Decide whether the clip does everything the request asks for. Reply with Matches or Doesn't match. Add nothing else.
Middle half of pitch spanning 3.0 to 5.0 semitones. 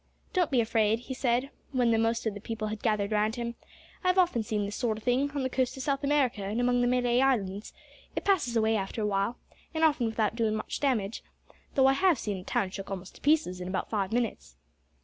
Matches